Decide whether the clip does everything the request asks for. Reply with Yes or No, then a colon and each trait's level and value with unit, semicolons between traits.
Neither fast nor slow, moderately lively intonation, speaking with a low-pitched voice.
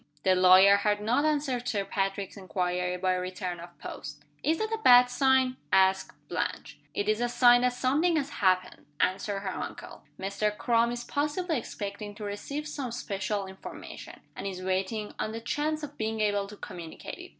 No: average, 180 wpm; average, 4.8 semitones; high, 210 Hz